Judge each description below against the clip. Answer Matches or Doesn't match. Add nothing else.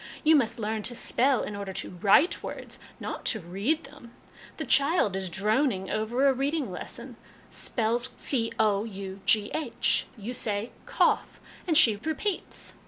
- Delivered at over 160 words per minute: Doesn't match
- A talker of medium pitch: Doesn't match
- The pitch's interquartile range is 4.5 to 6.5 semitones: Matches